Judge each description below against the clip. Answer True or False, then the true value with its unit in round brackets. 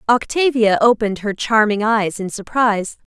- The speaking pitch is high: True (220 Hz)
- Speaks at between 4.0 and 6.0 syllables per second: True (5.0 syllables/s)